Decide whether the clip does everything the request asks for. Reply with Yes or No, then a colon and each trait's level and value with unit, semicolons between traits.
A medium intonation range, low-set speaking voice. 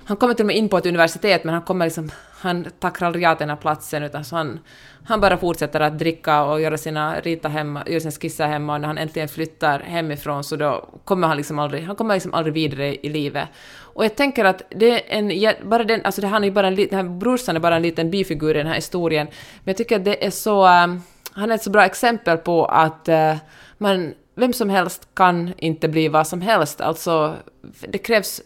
No: average, 4.1 semitones; medium, 170 Hz